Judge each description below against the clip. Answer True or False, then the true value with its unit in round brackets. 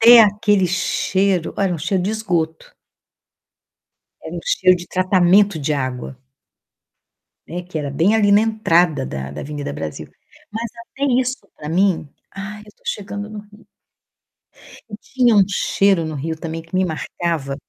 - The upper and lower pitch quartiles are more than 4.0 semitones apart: True (4.4 semitones)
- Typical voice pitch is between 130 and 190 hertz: True (185 Hz)